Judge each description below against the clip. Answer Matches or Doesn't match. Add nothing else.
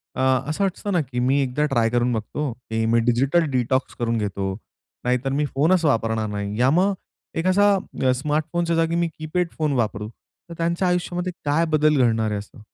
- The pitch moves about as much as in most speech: Doesn't match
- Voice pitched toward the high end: Doesn't match